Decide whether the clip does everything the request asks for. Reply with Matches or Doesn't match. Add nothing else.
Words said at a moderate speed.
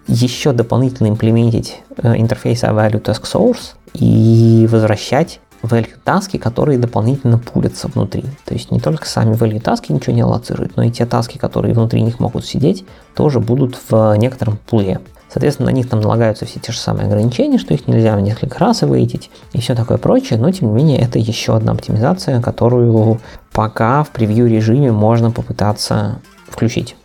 Doesn't match